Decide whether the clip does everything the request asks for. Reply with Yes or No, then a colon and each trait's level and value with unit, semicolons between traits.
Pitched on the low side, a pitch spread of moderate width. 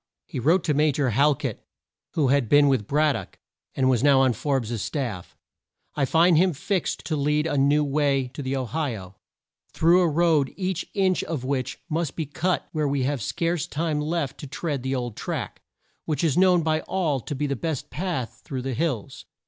No: medium, 145 Hz; average, 3.6 semitones